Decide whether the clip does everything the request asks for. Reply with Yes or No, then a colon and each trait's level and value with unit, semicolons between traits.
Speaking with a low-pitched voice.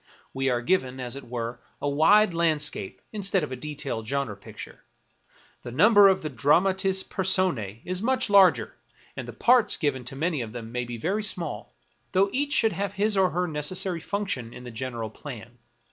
No: medium, 150 Hz